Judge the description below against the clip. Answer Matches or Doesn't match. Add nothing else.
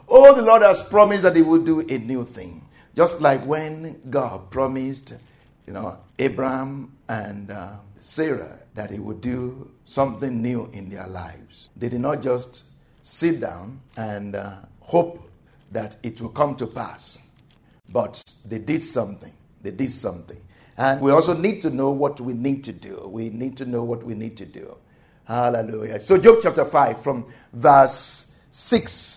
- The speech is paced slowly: Doesn't match